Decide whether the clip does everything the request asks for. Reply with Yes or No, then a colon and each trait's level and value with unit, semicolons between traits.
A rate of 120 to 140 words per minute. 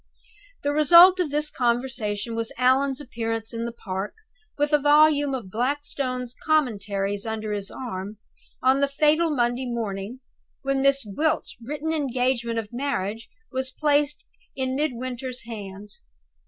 Yes: slow, 135 wpm